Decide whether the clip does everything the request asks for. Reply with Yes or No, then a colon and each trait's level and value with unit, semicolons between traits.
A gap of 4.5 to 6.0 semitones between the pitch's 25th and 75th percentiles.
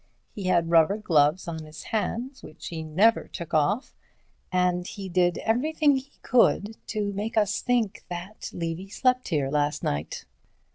Yes: average, 5.2 semitones